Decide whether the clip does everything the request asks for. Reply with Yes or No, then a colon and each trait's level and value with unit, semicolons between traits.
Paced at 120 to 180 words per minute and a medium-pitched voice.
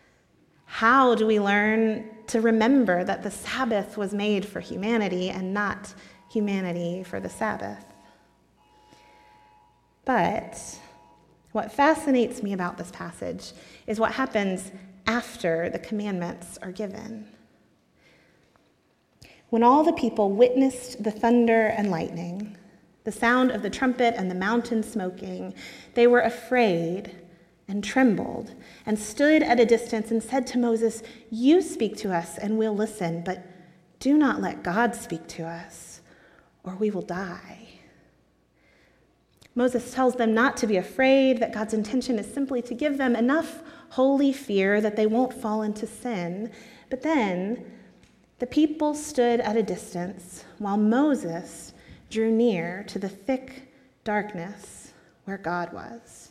No: slow, 135 wpm; high, 220 Hz